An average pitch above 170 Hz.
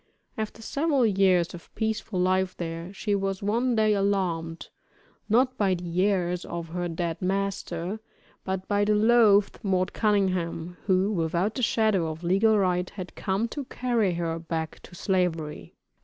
Yes: high, 190 Hz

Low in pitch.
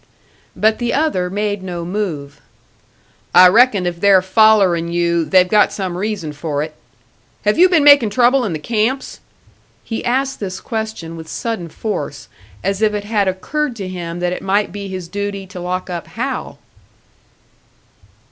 No: high, 195 Hz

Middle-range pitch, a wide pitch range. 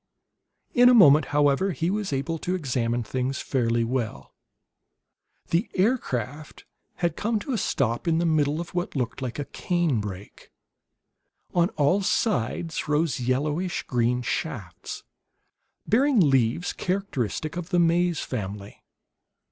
Yes: medium, 150 Hz; wide, 6.1 semitones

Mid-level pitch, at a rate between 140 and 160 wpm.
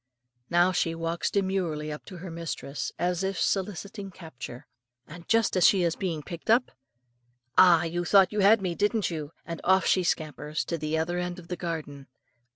No: medium, 175 Hz; average, 185 wpm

